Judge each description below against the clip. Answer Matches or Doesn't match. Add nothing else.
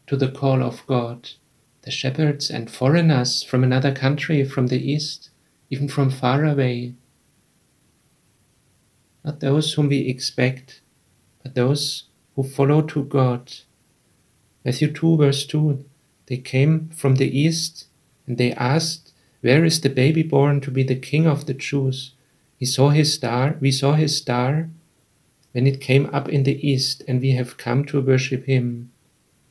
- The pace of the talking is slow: Doesn't match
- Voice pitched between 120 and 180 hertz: Matches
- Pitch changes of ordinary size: Doesn't match